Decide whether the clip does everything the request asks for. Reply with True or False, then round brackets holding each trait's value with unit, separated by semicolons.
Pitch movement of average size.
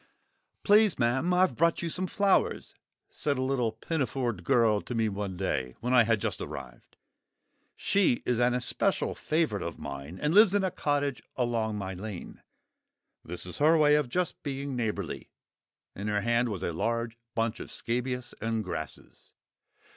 False (5.8 semitones)